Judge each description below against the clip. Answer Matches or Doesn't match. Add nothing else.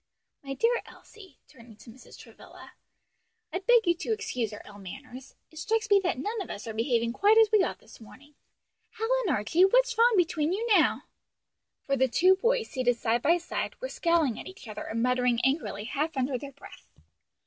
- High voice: Matches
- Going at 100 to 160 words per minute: Doesn't match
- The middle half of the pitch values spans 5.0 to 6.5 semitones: Doesn't match